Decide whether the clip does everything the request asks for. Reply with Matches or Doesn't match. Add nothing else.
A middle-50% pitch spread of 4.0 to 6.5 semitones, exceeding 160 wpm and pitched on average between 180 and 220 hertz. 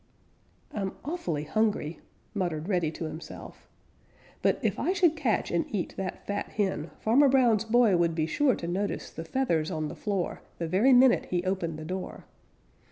Matches